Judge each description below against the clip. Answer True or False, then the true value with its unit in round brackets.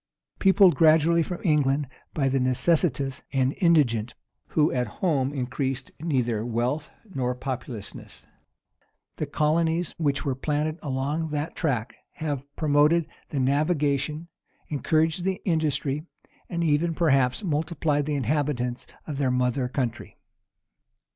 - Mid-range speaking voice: True (145 Hz)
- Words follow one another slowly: True (120 wpm)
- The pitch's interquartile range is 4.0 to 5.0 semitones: False (3.4 semitones)